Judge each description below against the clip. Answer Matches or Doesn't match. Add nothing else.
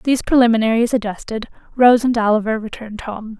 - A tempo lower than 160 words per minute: Matches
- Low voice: Doesn't match